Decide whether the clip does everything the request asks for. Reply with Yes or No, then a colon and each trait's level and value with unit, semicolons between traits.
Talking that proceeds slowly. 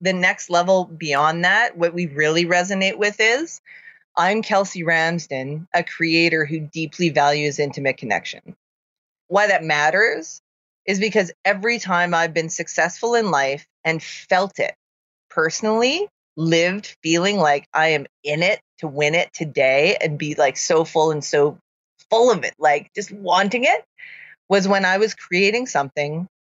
No: average, 155 wpm